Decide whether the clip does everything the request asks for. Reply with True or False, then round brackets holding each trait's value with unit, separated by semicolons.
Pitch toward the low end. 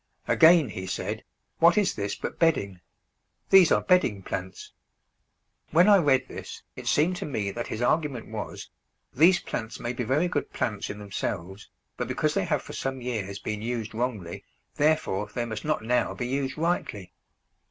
True (125 Hz)